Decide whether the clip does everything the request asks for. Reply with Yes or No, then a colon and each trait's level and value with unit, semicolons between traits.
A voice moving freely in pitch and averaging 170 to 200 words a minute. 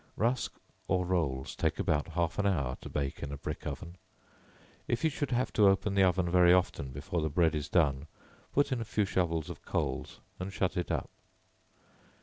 No: average, 4.4 semitones; average, 195 wpm